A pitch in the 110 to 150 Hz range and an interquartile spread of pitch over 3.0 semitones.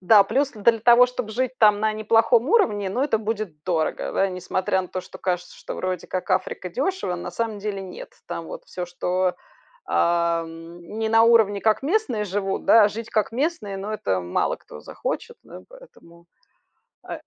No: high, 210 Hz; average, 4.1 semitones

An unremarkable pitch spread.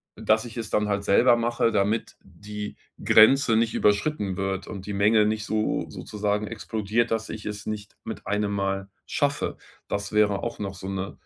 No: narrow, 1.7 semitones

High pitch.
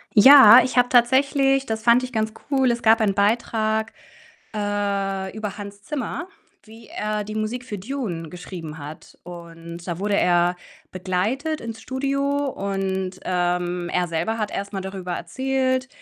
Yes: high, 210 Hz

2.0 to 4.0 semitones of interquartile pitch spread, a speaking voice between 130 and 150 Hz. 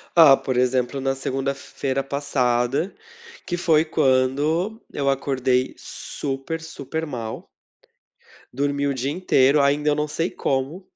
Yes: narrow, 2.5 semitones; medium, 140 Hz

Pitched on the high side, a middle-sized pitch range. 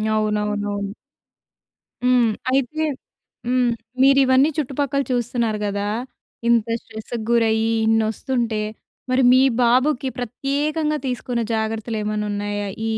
Yes: high, 235 Hz; average, 3.3 semitones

